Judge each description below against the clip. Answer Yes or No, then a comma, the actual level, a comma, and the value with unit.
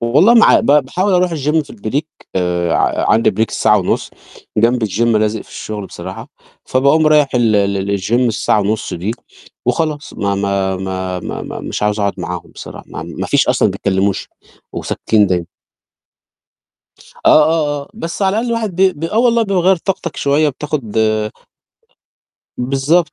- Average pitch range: No, wide, 8.1 semitones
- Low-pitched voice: Yes, low, 125 Hz